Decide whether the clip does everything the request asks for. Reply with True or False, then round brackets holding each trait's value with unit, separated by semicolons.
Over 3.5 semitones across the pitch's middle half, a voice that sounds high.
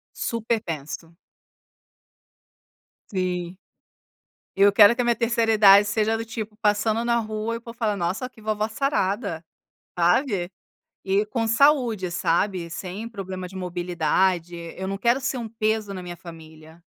True (4.1 semitones; 205 Hz)